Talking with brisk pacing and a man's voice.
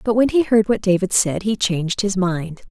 No: fast, 245 wpm; female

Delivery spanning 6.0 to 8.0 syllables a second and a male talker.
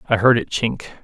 Yes: 6.1 syllables/s; male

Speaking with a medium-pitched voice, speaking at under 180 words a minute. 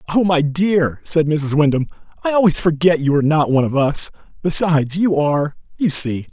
No: medium, 155 Hz; average, 190 wpm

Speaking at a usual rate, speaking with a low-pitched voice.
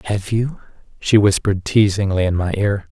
Yes: average, 160 wpm; low, 100 Hz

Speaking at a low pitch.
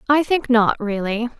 No: high, 240 Hz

